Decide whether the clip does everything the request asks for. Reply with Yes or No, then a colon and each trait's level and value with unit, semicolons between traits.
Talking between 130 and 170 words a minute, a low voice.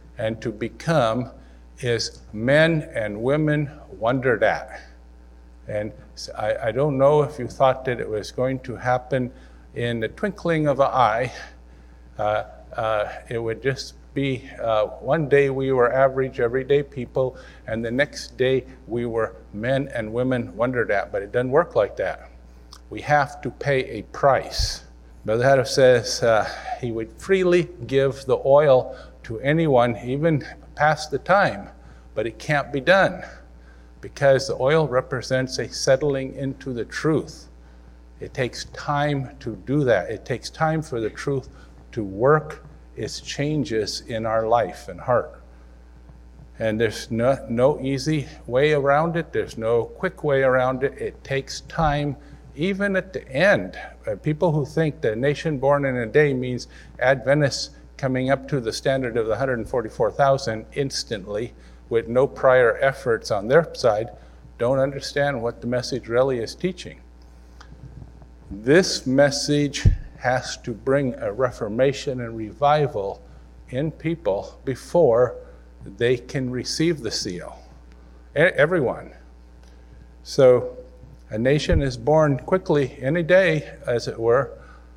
Yes: average, 145 wpm; low, 130 Hz